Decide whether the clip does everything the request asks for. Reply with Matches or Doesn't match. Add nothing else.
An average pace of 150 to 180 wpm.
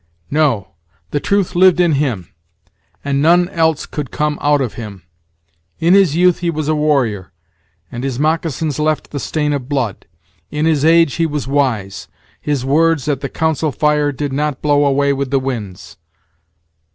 Matches